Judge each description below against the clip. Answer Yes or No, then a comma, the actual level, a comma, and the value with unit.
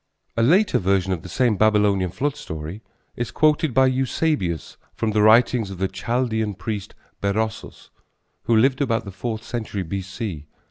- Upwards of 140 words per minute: Yes, average, 155 wpm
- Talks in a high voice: No, low, 110 Hz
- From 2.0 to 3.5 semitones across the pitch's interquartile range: No, average, 4.3 semitones